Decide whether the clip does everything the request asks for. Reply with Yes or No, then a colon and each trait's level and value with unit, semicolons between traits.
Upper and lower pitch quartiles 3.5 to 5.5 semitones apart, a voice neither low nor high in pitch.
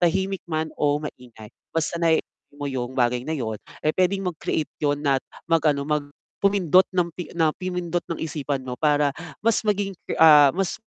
Yes: average, 3.8 semitones; medium, 155 Hz